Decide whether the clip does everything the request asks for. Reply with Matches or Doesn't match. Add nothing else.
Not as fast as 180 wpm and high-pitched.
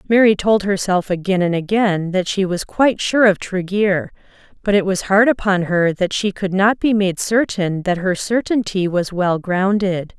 Doesn't match